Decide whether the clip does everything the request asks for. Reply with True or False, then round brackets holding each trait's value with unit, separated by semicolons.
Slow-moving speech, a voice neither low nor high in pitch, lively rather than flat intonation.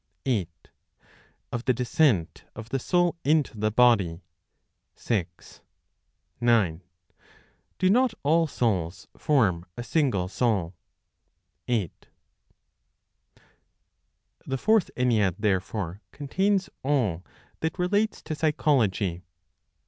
False (95 wpm; 120 Hz; 8.1 semitones)